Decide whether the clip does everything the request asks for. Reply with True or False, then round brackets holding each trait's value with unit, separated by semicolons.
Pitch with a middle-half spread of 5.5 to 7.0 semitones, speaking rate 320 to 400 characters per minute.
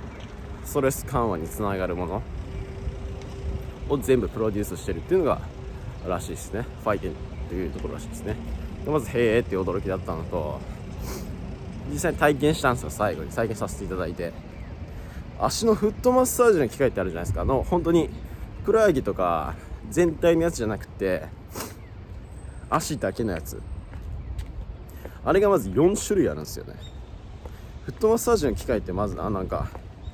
False (5.1 semitones; 350 characters per minute)